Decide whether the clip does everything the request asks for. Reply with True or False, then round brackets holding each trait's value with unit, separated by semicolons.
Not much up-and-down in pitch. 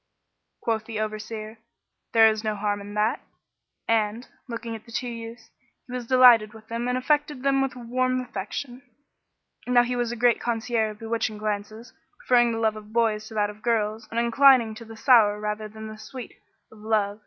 True (2.1 semitones)